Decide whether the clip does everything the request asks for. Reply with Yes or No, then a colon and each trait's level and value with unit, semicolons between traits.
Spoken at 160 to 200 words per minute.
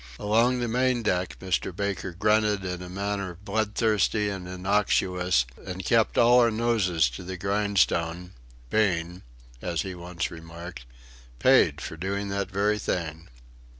No: average, 140 wpm